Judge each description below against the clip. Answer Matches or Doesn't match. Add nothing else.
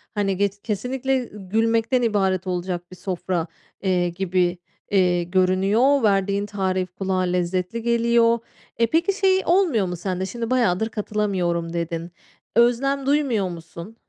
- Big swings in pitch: Doesn't match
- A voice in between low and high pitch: Doesn't match